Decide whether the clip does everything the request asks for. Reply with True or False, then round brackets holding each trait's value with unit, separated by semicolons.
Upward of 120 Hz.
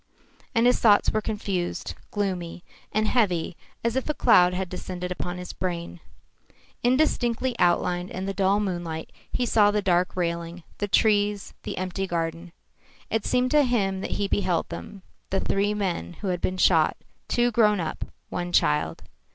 True (190 Hz)